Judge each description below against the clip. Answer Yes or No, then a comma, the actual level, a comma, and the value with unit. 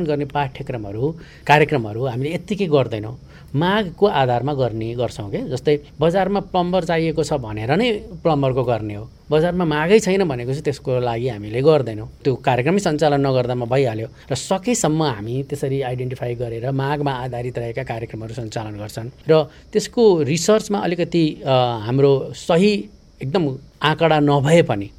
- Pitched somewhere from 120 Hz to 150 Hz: Yes, medium, 140 Hz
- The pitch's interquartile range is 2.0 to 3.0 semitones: No, average, 4.8 semitones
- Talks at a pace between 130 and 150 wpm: Yes, slow, 135 wpm